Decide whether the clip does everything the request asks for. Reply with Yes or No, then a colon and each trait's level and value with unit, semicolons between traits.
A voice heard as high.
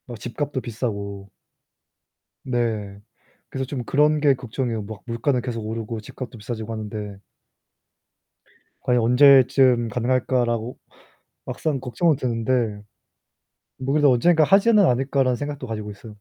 No: low, 125 Hz